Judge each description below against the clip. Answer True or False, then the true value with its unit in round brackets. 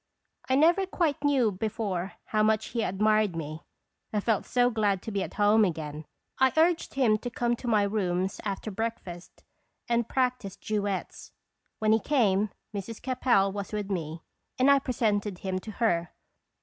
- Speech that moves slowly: False (165 wpm)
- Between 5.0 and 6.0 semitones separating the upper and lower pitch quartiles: False (3.9 semitones)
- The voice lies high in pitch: True (215 Hz)